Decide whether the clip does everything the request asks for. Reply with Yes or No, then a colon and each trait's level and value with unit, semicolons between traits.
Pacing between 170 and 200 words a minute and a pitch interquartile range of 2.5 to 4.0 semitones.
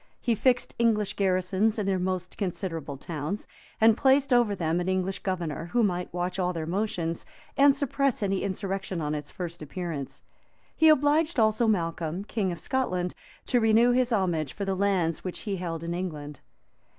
No: average, 175 wpm; average, 4.5 semitones